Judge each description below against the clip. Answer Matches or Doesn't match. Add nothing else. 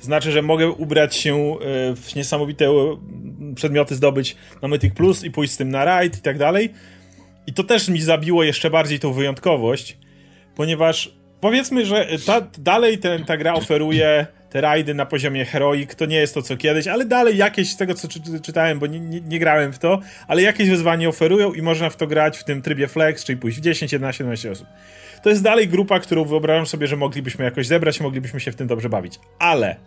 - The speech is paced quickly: Matches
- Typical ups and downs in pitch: Matches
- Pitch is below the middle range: Doesn't match